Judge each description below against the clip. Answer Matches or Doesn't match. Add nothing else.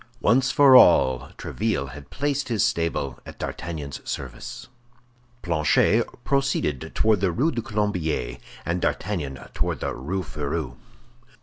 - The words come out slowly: Matches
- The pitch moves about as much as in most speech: Doesn't match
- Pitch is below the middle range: Matches